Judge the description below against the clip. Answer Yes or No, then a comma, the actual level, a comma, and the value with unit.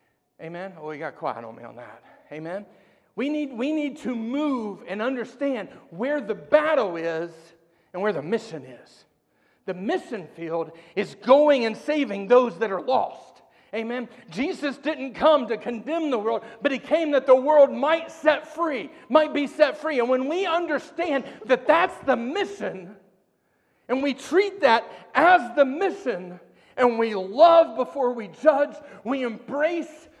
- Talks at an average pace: Yes, average, 165 wpm